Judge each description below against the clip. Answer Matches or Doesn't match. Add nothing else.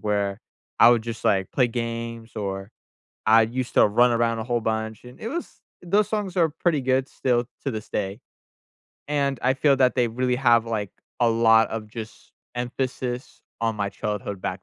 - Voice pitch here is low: Matches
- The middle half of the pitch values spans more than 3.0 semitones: Doesn't match